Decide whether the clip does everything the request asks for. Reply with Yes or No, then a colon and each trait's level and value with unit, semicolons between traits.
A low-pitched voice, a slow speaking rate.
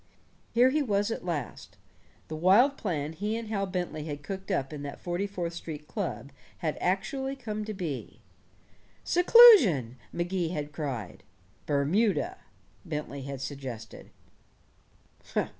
No: medium, 175 Hz; slow, 130 wpm